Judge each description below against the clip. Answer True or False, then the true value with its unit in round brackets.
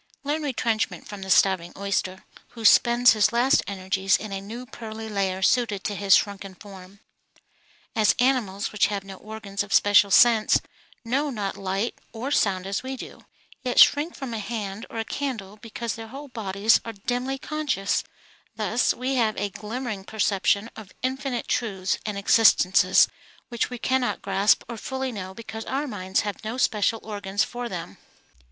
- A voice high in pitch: True (215 Hz)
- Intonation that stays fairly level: False (3.6 semitones)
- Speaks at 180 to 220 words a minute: False (165 wpm)